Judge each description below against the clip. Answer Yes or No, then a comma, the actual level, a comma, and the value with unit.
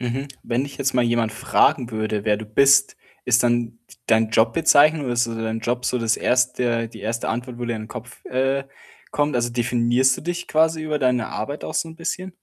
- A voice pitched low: Yes, low, 125 Hz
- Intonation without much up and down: No, average, 3.1 semitones